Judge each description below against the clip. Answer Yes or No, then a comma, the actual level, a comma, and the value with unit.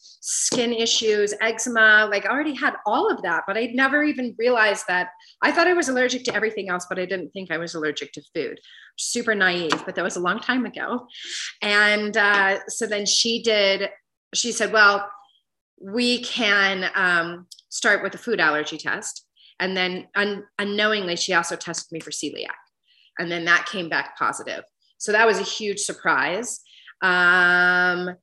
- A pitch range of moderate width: Yes, average, 3.9 semitones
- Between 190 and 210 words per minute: No, average, 175 wpm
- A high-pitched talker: Yes, high, 205 Hz